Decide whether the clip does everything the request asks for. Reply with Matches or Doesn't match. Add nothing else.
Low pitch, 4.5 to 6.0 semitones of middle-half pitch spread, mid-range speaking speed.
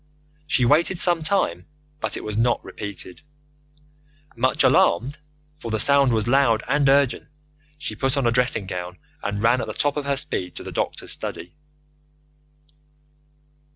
Matches